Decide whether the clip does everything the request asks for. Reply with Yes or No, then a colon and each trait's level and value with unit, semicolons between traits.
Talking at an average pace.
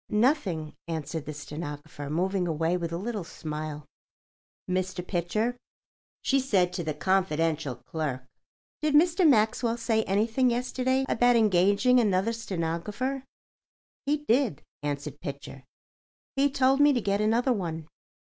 No: slow, 130 wpm